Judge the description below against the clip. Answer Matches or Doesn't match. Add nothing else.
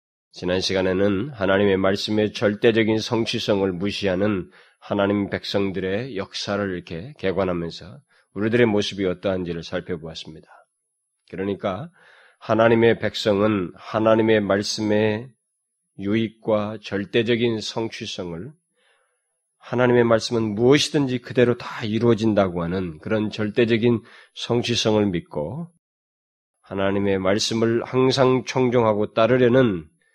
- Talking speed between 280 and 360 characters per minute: Matches